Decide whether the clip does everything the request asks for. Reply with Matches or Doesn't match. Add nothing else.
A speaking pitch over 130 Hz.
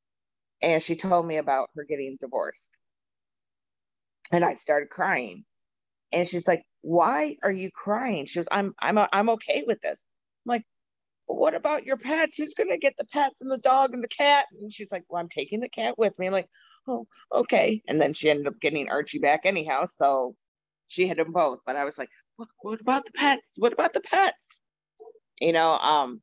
Matches